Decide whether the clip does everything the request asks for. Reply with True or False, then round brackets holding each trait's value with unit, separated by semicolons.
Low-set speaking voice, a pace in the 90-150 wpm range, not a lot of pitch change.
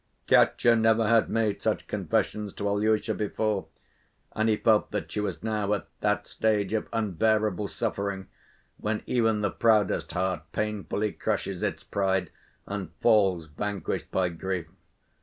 True (105 Hz; 140 wpm; 2.0 semitones)